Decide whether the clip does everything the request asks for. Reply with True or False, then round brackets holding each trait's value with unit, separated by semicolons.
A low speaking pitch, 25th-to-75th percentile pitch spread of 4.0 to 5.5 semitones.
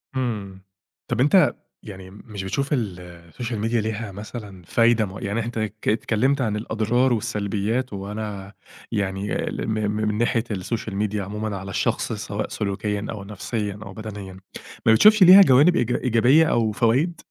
False (110 Hz; 3.0 semitones)